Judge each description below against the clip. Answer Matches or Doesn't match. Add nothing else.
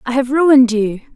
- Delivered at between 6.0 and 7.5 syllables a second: Doesn't match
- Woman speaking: Matches